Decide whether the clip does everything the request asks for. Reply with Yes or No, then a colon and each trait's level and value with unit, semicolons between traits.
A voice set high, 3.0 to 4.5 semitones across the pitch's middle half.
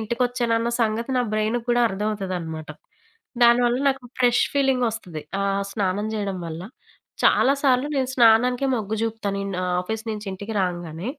Yes: high, 220 Hz; average, 3.7 semitones